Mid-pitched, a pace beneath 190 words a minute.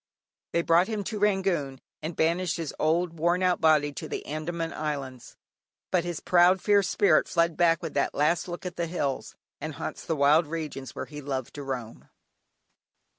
Yes: medium, 165 Hz; average, 180 wpm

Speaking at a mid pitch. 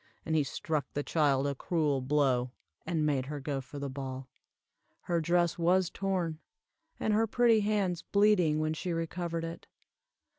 Yes: medium, 160 Hz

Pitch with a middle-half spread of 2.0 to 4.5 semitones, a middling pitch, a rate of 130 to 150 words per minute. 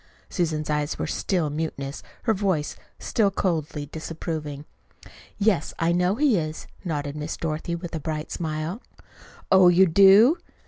Yes: average, 3.7 semitones; medium, 165 Hz; average, 140 wpm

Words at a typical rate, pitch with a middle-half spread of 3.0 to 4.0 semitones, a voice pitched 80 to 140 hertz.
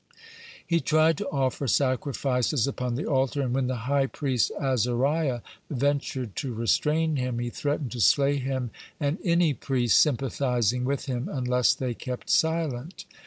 No: average, 155 wpm; narrow, 2.6 semitones; low, 135 Hz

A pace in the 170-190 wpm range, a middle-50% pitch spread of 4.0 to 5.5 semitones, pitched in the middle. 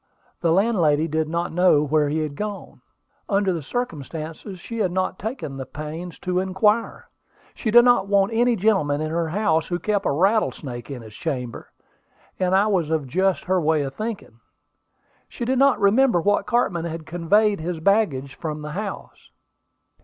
Yes: average, 175 wpm; average, 5.0 semitones; medium, 175 Hz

